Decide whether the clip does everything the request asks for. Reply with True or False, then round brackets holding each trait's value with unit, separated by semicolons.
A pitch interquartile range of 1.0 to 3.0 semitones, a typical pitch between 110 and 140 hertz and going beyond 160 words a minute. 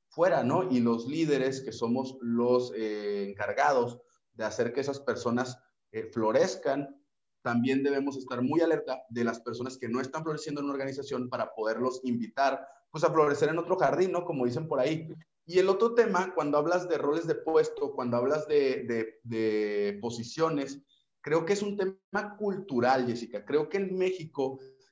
False (5.4 semitones; 135 Hz; 175 wpm)